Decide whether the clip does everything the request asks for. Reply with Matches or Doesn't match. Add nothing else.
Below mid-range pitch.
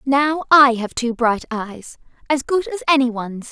Doesn't match